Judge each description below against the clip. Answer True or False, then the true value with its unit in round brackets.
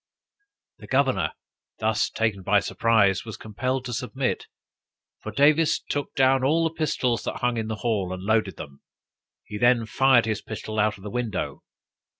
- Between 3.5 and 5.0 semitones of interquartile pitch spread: True (3.9 semitones)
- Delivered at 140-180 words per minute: True (165 wpm)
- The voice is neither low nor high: False (115 Hz)